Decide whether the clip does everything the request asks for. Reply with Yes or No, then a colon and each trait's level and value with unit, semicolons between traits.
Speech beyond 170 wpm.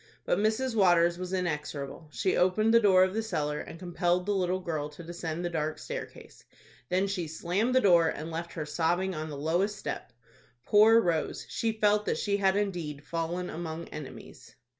Yes: average, 185 wpm